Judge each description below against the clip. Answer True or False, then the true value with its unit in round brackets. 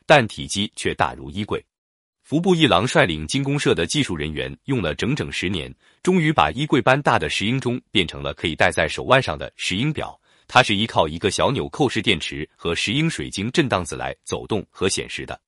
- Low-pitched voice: True (110 Hz)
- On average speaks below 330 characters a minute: True (310 characters per minute)